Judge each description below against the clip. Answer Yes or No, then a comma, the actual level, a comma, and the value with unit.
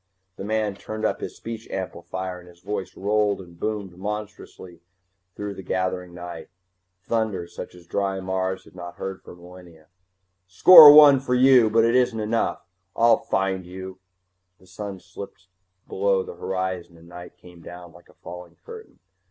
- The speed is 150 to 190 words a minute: Yes, average, 165 wpm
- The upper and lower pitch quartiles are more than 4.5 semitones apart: No, average, 3.2 semitones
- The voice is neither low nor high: No, very low, 95 Hz